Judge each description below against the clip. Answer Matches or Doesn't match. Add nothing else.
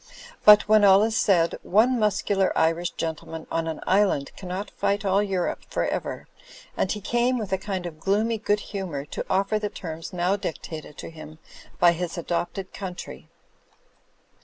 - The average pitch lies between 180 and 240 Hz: Matches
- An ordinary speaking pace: Matches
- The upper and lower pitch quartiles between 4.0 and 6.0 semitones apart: Doesn't match